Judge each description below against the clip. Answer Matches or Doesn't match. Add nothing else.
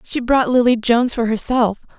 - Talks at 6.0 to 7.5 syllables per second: Doesn't match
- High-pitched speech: Matches